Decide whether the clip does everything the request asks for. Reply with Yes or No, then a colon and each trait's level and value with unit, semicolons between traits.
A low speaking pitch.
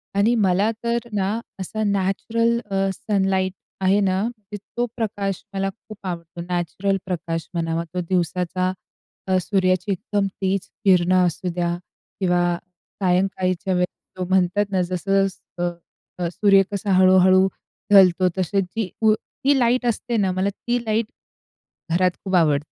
No: high, 190 Hz